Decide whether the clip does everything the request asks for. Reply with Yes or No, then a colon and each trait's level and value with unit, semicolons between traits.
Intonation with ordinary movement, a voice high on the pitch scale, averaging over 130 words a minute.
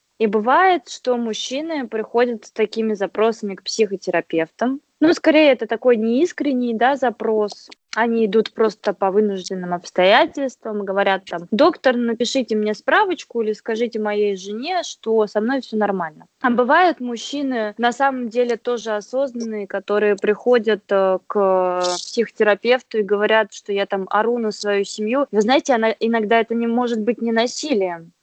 Yes: average, 3.2 semitones; high, 225 Hz; average, 145 wpm